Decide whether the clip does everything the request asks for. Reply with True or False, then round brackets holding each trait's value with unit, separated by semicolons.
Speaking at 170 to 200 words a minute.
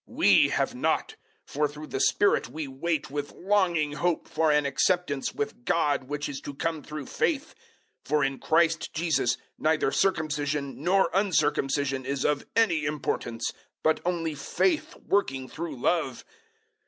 False (155 wpm)